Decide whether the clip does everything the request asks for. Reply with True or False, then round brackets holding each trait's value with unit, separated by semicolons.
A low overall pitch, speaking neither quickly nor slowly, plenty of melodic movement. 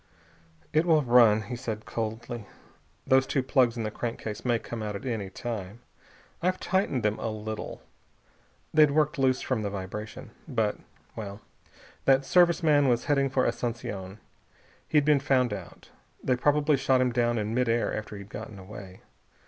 False (120 Hz; 165 wpm; 3.9 semitones)